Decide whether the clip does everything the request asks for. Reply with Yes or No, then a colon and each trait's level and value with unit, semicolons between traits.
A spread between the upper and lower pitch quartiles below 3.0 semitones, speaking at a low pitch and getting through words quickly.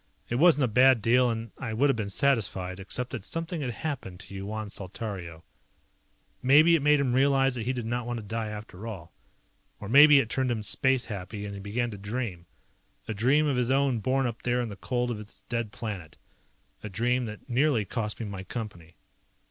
No: average, 4.1 semitones; low, 115 Hz; fast, 210 wpm